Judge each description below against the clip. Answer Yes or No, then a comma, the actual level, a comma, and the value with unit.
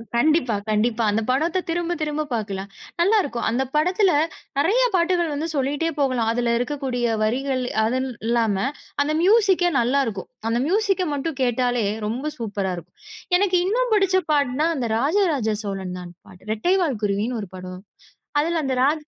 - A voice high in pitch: Yes, very high, 265 Hz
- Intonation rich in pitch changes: Yes, wide, 6.7 semitones